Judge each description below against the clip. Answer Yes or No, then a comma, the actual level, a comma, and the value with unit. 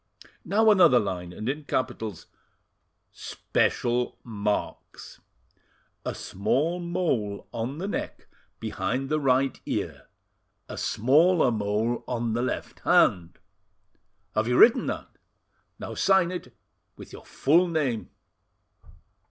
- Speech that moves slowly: Yes, slow, 110 wpm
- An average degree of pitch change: No, wide, 7.3 semitones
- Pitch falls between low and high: No, low, 125 Hz